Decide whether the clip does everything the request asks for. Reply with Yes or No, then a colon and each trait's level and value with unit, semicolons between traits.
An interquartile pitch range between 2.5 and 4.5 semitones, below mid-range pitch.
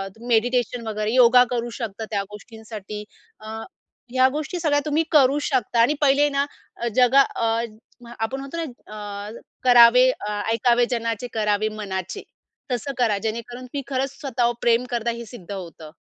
No: average, 2.9 semitones; high, 235 Hz